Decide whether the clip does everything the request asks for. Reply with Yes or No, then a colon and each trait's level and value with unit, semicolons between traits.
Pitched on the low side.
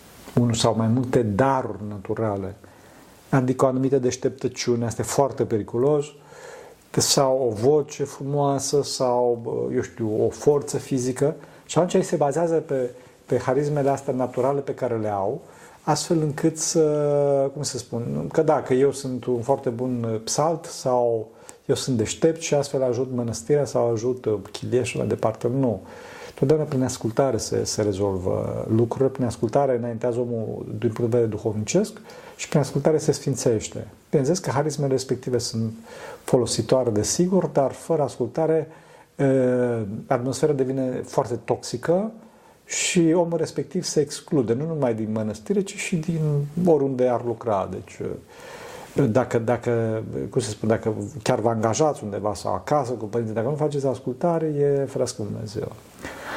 Yes: low, 130 Hz